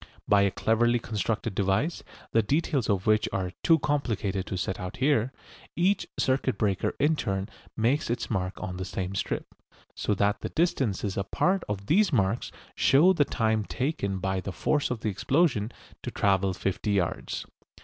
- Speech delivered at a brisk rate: No, average, 170 wpm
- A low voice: Yes, low, 110 Hz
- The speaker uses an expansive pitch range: Yes, wide, 5.7 semitones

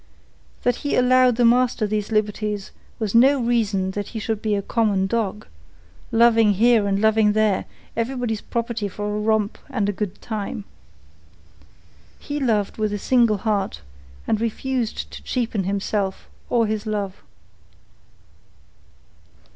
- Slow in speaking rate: Yes, slow, 130 wpm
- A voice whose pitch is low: No, high, 215 Hz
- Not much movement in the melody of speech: Yes, narrow, 2.3 semitones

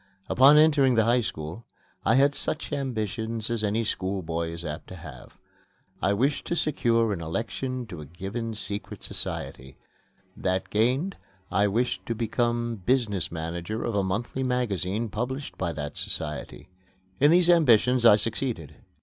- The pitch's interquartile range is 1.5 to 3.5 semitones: No, average, 5.2 semitones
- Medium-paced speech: Yes, average, 150 wpm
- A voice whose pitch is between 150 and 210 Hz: No, low, 110 Hz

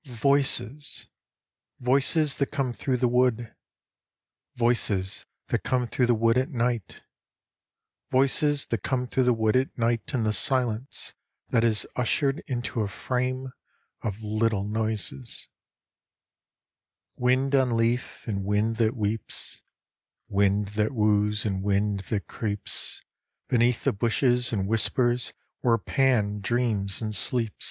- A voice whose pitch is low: Yes, low, 115 Hz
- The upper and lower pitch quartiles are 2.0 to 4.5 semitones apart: Yes, average, 3.2 semitones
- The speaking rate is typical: No, slow, 130 wpm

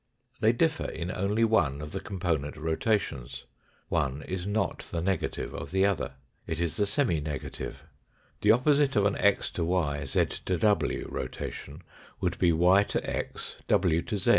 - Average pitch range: Yes, average, 4.7 semitones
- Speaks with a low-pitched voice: Yes, very low, 90 Hz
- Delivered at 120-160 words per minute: No, average, 170 wpm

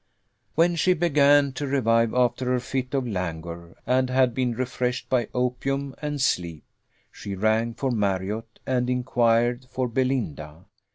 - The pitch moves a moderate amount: Yes, average, 3.0 semitones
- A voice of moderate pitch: No, low, 125 Hz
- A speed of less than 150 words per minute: Yes, average, 140 wpm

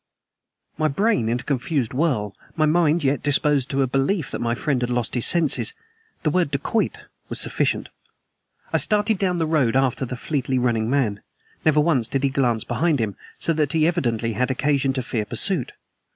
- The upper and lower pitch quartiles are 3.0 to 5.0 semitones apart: Yes, average, 4.3 semitones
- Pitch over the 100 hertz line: Yes, medium, 140 Hz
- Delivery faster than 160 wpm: Yes, average, 190 wpm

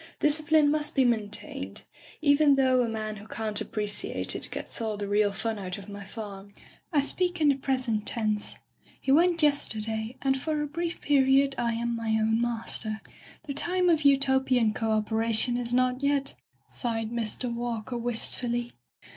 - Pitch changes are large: No, average, 4.2 semitones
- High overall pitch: Yes, high, 240 Hz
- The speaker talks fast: No, average, 165 wpm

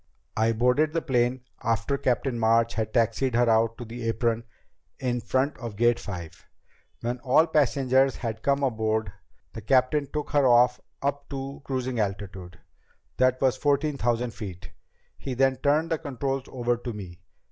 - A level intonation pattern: No, average, 3.0 semitones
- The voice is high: No, low, 125 Hz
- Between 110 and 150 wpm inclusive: No, average, 165 wpm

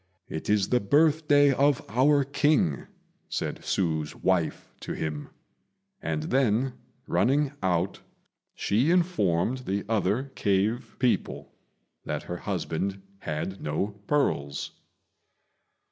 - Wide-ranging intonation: Yes, wide, 7.3 semitones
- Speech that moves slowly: Yes, slow, 105 wpm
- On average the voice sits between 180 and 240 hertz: No, low, 105 Hz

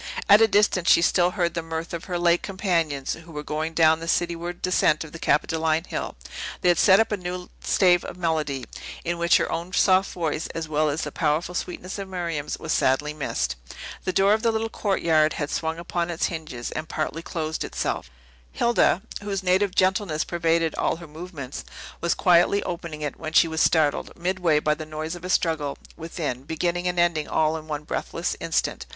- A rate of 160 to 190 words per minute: No, average, 200 wpm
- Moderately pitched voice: Yes, medium, 170 Hz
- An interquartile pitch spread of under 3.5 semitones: Yes, narrow, 2.4 semitones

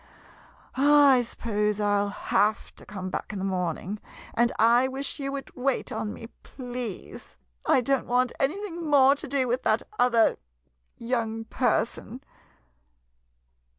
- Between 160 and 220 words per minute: No, average, 145 wpm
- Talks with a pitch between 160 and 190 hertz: No, high, 245 Hz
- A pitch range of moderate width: Yes, average, 4.2 semitones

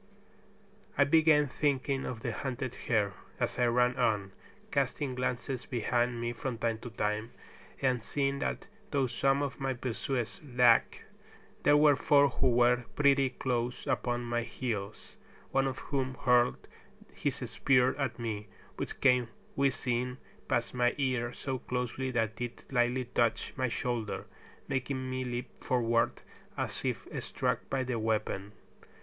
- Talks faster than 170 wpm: No, average, 145 wpm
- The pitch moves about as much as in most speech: No, narrow, 2.1 semitones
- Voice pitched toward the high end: No, low, 125 Hz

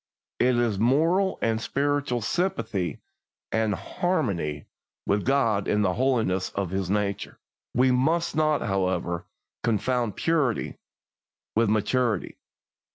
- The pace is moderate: No, slow, 110 wpm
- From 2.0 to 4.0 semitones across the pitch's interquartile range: No, wide, 5.5 semitones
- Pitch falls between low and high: No, low, 115 Hz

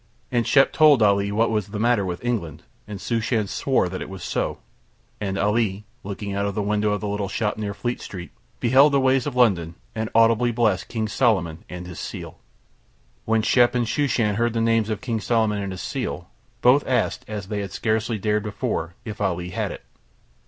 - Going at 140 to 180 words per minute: No, average, 200 wpm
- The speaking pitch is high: No, low, 105 Hz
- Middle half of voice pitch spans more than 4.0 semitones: No, average, 3.0 semitones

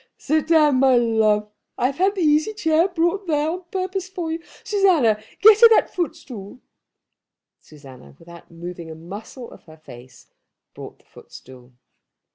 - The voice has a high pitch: Yes, very high, 280 Hz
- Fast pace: No, average, 155 wpm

